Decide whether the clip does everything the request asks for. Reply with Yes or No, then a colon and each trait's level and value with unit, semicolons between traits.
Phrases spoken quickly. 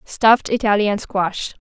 No: slow, 110 wpm